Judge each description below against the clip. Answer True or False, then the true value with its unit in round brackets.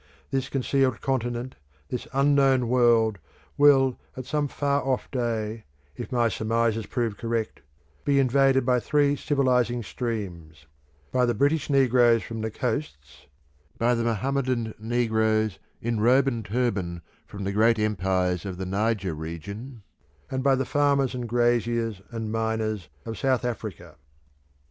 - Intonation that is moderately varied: True (3.3 semitones)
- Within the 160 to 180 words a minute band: False (140 wpm)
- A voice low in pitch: True (120 Hz)